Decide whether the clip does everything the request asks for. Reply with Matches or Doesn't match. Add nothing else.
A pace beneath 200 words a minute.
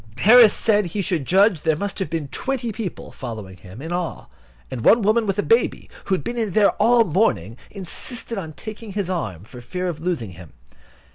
Doesn't match